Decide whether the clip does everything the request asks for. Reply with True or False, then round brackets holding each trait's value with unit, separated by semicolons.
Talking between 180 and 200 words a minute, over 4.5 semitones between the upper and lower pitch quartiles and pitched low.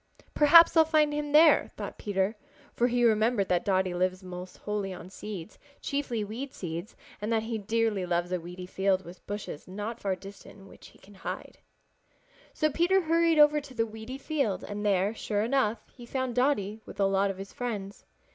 False (195 wpm; 5.2 semitones; 210 Hz)